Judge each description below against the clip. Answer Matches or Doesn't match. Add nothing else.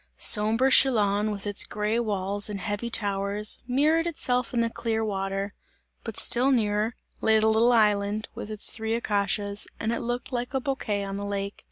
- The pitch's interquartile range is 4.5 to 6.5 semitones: Doesn't match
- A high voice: Matches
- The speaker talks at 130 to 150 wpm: Doesn't match